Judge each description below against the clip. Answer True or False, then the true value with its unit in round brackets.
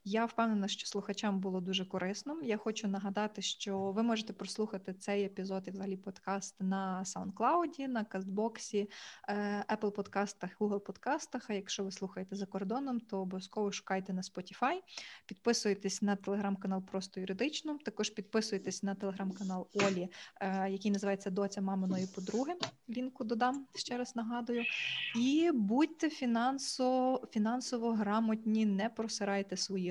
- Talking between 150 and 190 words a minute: False (130 wpm)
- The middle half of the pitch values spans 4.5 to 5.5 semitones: False (3.2 semitones)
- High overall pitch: True (205 Hz)